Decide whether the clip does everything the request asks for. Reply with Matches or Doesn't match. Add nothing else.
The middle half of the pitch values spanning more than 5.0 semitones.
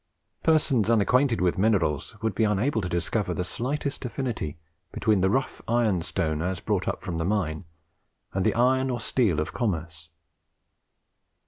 Matches